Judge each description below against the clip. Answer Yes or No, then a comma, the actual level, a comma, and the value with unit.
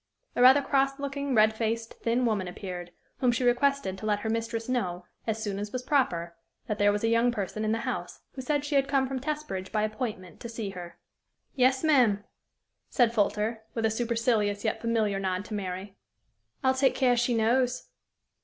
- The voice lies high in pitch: Yes, high, 230 Hz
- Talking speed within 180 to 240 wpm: Yes, average, 200 wpm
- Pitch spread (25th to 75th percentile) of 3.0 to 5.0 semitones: Yes, average, 3.8 semitones